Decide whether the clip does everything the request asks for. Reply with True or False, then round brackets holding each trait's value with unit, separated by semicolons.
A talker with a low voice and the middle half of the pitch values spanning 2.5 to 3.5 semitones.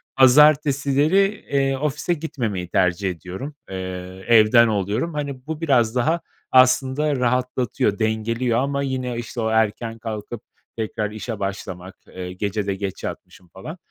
False (120 Hz; 4.8 semitones)